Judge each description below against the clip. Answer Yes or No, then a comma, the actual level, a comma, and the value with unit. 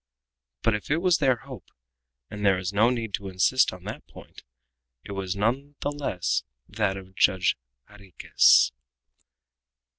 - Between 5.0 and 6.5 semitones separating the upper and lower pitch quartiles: Yes, average, 5.3 semitones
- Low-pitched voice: Yes, low, 105 Hz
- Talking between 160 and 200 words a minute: No, average, 150 wpm